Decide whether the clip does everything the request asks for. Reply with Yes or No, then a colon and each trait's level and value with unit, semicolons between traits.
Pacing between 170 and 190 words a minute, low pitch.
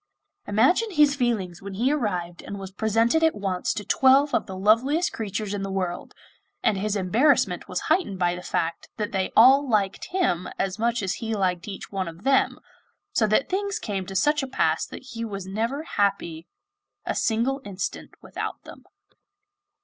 No: average, 180 wpm; high, 210 Hz